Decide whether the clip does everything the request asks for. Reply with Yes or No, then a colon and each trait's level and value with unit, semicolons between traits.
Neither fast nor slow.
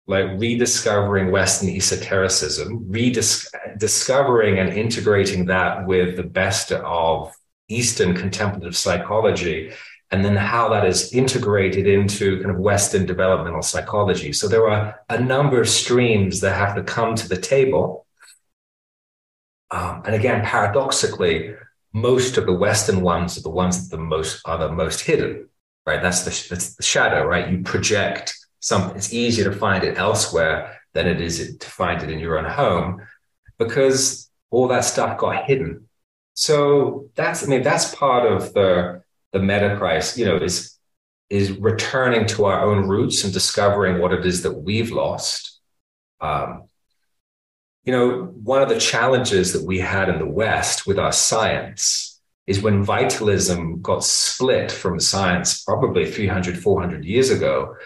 Yes: average, 155 wpm